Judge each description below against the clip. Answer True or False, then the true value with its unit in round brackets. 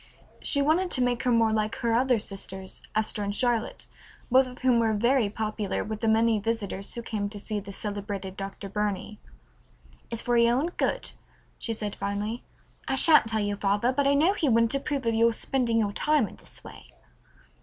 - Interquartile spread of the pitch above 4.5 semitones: False (3.4 semitones)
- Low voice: False (225 Hz)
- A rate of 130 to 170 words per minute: False (195 wpm)